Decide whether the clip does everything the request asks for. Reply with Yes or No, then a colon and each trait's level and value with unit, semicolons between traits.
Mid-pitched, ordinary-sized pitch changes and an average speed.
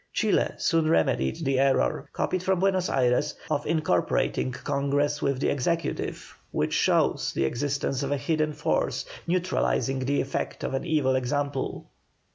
Yes: medium, 145 Hz; average, 3.1 semitones; average, 145 wpm